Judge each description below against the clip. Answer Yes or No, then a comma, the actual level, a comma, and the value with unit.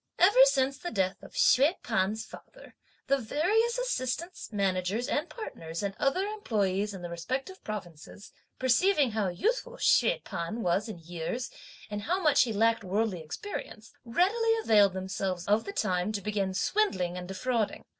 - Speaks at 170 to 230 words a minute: No, average, 155 wpm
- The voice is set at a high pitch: Yes, high, 220 Hz